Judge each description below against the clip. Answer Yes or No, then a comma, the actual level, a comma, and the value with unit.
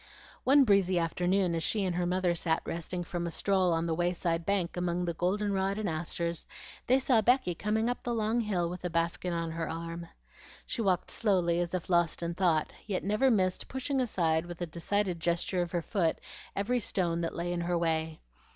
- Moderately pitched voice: Yes, medium, 175 Hz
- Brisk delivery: Yes, fast, 210 wpm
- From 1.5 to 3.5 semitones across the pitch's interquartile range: Yes, average, 2.9 semitones